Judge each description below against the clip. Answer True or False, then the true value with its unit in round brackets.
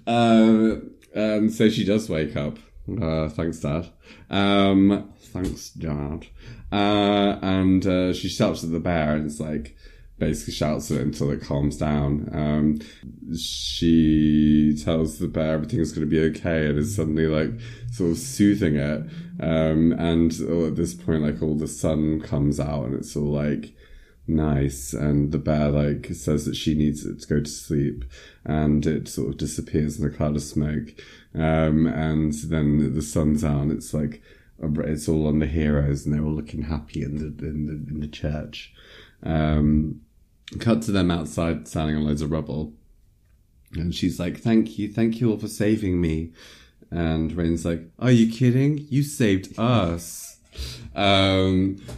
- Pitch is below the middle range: True (80 Hz)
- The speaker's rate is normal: True (170 wpm)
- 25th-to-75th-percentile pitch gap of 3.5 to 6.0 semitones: True (3.9 semitones)